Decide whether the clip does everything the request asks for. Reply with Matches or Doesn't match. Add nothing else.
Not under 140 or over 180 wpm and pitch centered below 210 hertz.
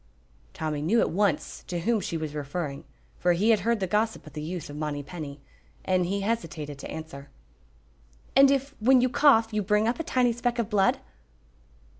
Doesn't match